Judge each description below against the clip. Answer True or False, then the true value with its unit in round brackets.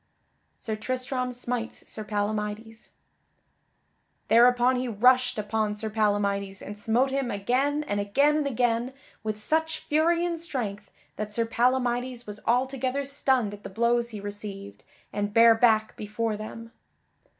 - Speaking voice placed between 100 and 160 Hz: False (230 Hz)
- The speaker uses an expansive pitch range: False (3.4 semitones)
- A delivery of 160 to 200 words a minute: False (140 wpm)